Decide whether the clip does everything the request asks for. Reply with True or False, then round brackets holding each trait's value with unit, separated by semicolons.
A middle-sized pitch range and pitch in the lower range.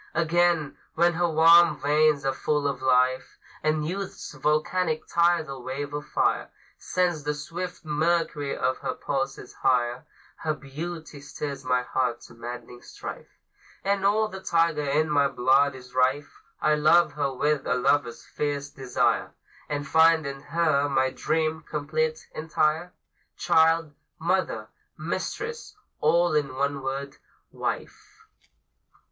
False (3.1 semitones; 150 Hz)